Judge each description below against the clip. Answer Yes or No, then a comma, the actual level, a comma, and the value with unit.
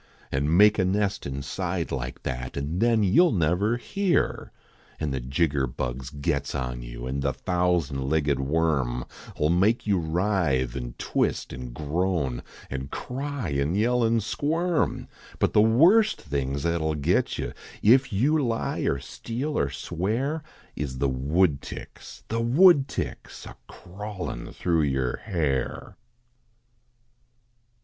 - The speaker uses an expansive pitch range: Yes, wide, 8.2 semitones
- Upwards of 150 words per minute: No, average, 140 wpm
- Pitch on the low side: Yes, very low, 85 Hz